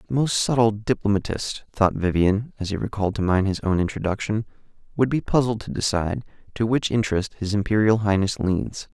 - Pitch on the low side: Yes, low, 105 Hz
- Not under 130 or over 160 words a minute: No, average, 175 wpm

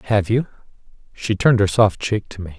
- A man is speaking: Yes, male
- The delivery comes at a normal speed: No, fast, 210 wpm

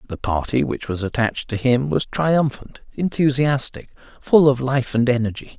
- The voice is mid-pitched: No, low, 130 Hz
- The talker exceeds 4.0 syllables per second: Yes, 4.9 syllables/s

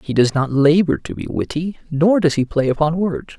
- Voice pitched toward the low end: No, medium, 160 Hz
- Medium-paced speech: No, fast, 230 wpm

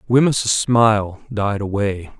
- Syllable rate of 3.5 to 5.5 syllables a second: Yes, 3.7 syllables/s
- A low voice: Yes, low, 110 Hz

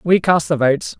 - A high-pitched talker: No, medium, 160 Hz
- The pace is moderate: No, fast, 240 wpm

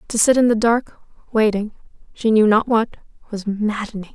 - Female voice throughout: Yes, female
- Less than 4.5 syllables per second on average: No, 5.0 syllables/s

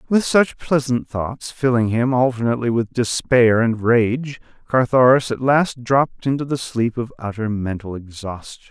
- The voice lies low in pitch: Yes, low, 120 Hz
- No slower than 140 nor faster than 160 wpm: Yes, average, 150 wpm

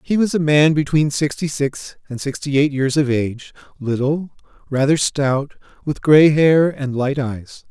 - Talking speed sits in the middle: Yes, average, 170 wpm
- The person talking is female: No, male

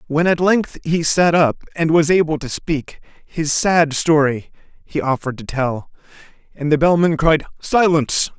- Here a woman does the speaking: No, male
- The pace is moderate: Yes, average, 165 wpm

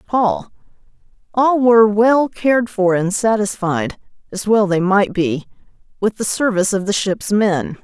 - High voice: Yes, high, 205 Hz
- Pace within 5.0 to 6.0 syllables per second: No, 4.4 syllables/s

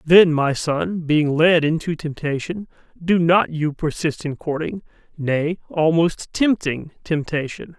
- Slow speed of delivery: Yes, slow, 130 wpm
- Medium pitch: Yes, medium, 160 Hz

